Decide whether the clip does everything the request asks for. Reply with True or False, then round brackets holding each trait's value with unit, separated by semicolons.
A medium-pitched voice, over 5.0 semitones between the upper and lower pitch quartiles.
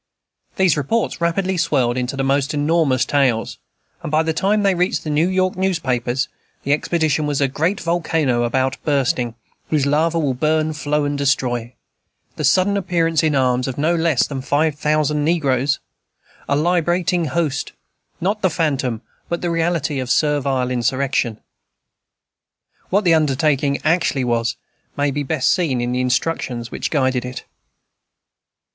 False (145 Hz; 4.2 semitones)